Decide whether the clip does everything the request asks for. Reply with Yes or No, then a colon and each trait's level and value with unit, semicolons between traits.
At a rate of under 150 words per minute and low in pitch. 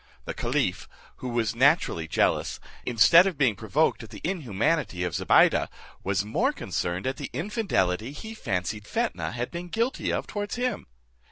No: average, 160 wpm; low, 125 Hz